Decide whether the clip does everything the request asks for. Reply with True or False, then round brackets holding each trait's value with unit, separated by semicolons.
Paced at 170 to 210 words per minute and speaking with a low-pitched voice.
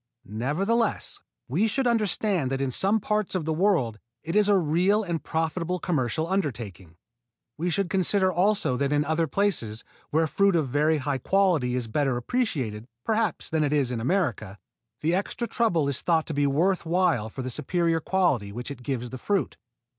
False (180 wpm; 160 Hz)